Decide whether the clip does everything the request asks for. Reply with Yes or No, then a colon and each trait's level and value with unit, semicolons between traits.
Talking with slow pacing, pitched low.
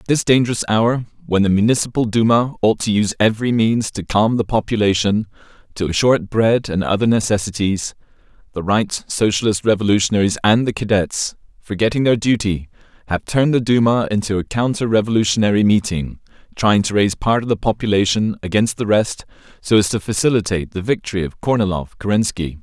No: average, 165 wpm; low, 105 Hz